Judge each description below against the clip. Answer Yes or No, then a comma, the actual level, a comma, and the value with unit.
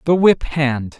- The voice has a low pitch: No, medium, 150 Hz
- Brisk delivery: No, average, 180 wpm